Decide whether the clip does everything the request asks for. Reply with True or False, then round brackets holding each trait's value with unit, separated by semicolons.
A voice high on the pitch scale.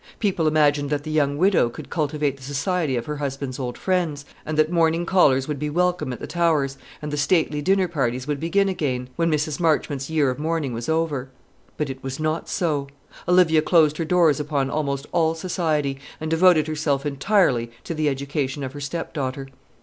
False (150 Hz)